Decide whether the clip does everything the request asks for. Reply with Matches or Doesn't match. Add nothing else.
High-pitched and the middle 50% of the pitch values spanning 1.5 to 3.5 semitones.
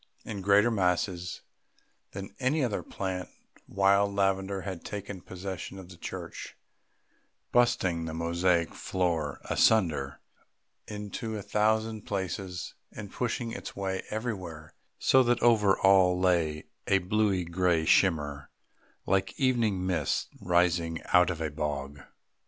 Doesn't match